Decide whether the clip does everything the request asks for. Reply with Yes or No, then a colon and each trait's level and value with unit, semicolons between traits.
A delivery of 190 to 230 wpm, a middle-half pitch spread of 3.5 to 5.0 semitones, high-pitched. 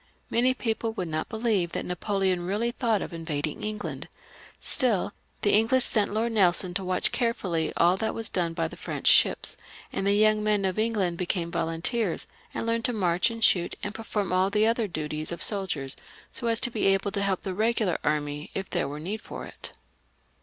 Yes: average, 200 wpm; average, 4.2 semitones; high, 195 Hz